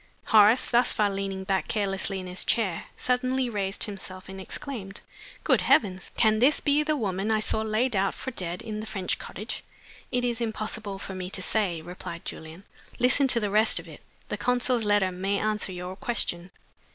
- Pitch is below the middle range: No, high, 205 Hz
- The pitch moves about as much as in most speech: Yes, average, 3.4 semitones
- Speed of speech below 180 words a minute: No, average, 190 wpm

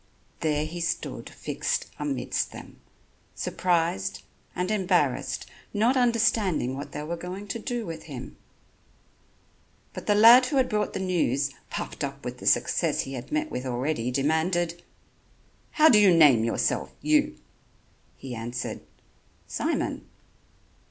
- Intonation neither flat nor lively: No, wide, 7.9 semitones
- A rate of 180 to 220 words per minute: No, slow, 135 wpm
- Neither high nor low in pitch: Yes, medium, 175 Hz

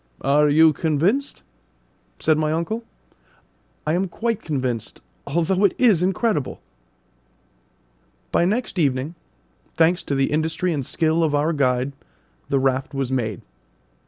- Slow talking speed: Yes, slow, 130 wpm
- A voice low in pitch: No, medium, 155 Hz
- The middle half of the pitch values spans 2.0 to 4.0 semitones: No, average, 4.5 semitones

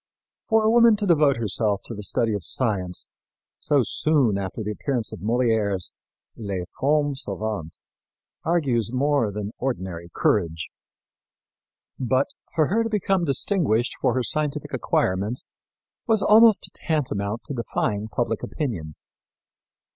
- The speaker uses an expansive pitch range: Yes, wide, 6.7 semitones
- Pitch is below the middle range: Yes, low, 120 Hz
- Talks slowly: Yes, slow, 130 wpm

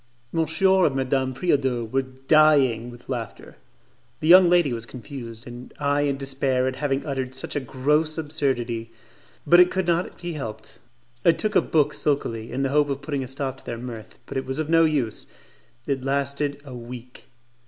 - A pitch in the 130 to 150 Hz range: Yes, low, 135 Hz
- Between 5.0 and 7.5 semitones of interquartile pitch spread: No, average, 3.2 semitones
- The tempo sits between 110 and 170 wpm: No, average, 185 wpm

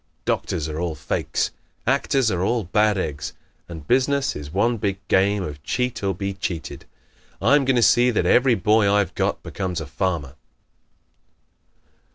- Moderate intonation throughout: No, wide, 6.1 semitones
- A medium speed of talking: Yes, average, 160 wpm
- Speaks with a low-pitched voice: Yes, low, 100 Hz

